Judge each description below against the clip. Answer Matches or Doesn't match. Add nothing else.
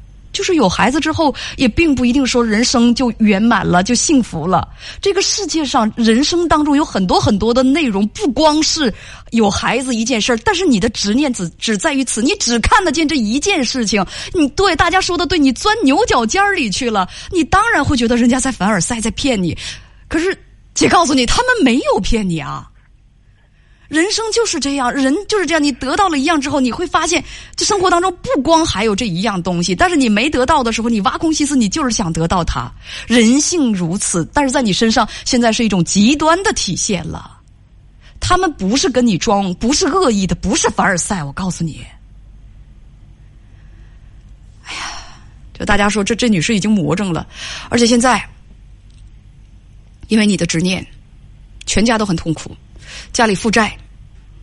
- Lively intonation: Matches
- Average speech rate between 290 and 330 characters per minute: Doesn't match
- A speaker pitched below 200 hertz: Doesn't match